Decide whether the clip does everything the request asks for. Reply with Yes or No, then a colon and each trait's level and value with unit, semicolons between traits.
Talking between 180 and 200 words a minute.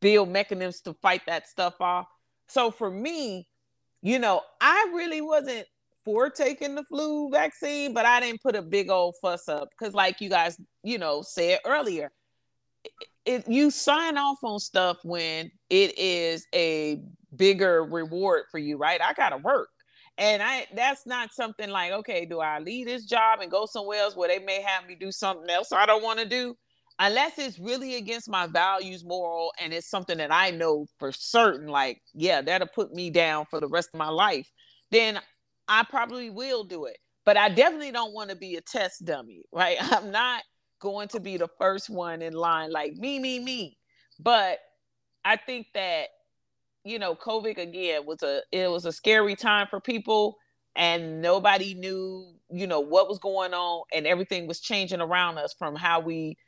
Yes: average, 190 wpm